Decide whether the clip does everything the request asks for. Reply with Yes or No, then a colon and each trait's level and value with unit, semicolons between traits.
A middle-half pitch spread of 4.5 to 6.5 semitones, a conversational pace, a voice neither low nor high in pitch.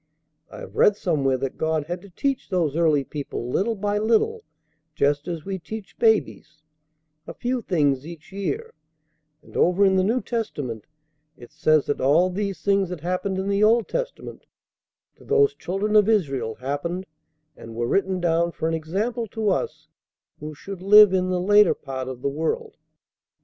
Yes: wide, 5.6 semitones; average, 175 wpm; medium, 180 Hz